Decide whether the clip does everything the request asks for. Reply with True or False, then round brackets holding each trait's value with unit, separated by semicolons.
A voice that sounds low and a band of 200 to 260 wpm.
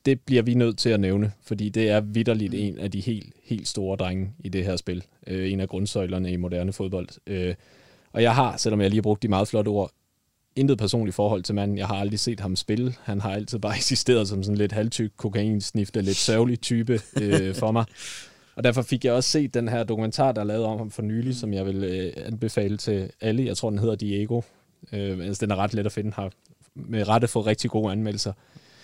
True (105 Hz; 225 wpm)